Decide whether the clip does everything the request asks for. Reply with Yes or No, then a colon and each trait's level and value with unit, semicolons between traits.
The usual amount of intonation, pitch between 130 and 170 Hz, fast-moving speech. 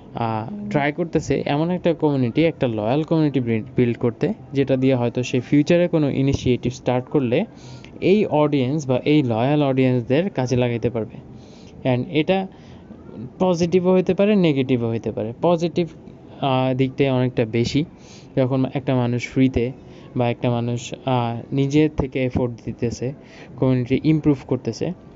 Yes: average, 3.6 semitones; low, 135 Hz; fast, 130 wpm